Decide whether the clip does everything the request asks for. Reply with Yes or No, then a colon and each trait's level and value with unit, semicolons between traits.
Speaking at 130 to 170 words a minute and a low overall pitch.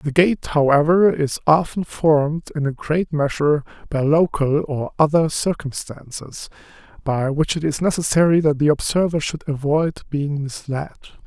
No: average, 145 wpm; medium, 150 Hz